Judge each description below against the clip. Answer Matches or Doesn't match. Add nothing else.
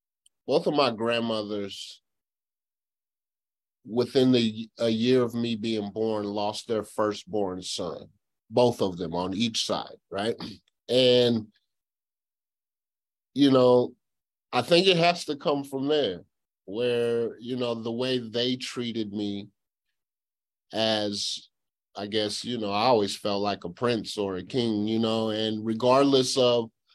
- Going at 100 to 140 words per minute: Matches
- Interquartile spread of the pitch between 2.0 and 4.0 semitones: Matches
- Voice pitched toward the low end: Matches